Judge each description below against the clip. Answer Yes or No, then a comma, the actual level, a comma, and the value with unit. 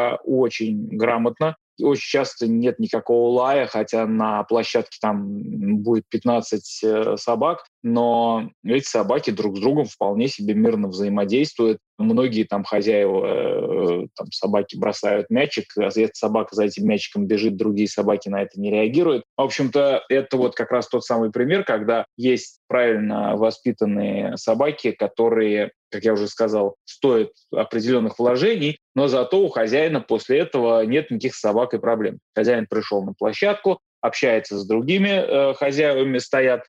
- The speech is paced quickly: No, average, 140 wpm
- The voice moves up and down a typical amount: Yes, average, 4.0 semitones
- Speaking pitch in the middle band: No, low, 115 Hz